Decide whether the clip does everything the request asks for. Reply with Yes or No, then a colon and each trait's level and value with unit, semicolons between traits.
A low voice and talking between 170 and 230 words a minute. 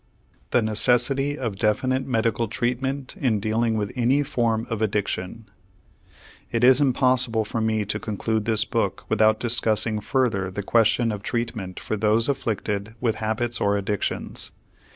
No: low, 115 Hz; average, 145 wpm